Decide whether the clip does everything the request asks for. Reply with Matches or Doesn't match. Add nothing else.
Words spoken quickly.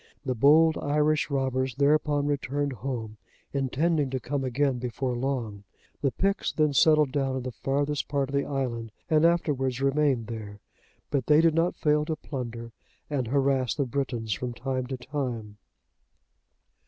Doesn't match